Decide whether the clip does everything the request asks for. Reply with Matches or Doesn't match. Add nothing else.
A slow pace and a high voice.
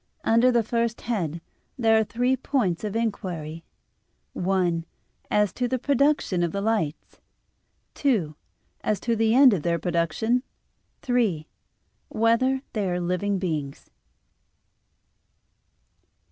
Matches